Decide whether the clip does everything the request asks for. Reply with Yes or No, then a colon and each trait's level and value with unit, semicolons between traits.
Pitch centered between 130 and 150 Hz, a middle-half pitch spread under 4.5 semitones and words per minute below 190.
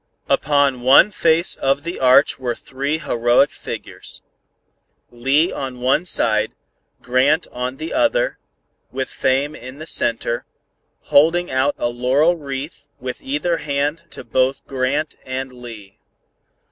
Yes: low, 135 Hz; average, 3.2 semitones; slow, 135 wpm